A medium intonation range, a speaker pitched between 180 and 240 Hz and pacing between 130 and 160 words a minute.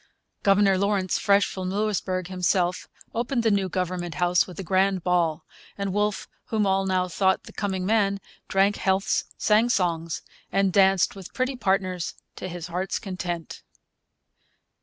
No: narrow, 1.7 semitones; high, 190 Hz; average, 150 wpm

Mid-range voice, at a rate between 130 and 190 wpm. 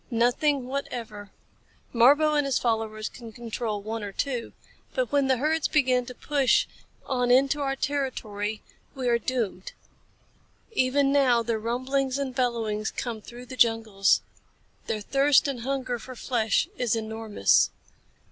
No: high, 245 Hz; average, 140 wpm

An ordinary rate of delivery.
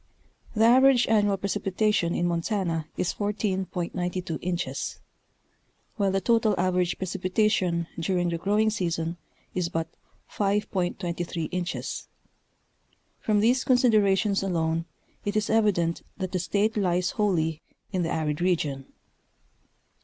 No: slow, 115 wpm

